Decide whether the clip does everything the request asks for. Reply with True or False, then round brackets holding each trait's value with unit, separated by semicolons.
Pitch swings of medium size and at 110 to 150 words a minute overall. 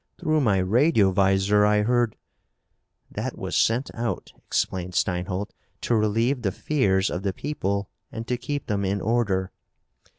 True (3.8 semitones; 145 wpm)